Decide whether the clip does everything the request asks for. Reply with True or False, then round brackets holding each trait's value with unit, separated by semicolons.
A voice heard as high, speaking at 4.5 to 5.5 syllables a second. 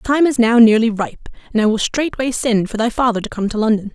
False (230 Hz; 6.1 syllables/s)